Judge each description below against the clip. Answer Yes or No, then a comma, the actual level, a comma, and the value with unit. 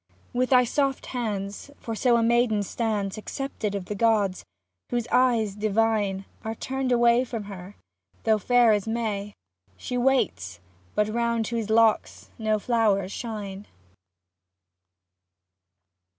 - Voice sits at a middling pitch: No, high, 220 Hz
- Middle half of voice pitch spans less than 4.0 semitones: Yes, average, 2.8 semitones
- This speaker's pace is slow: Yes, slow, 130 wpm